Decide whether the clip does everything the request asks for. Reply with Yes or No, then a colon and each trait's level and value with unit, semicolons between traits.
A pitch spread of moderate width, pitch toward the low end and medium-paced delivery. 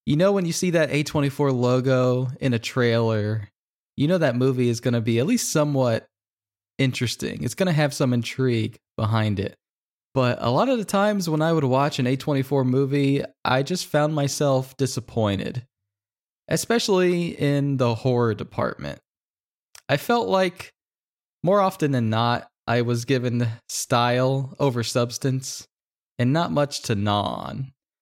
Yes: average, 3.7 semitones; low, 130 Hz; average, 155 wpm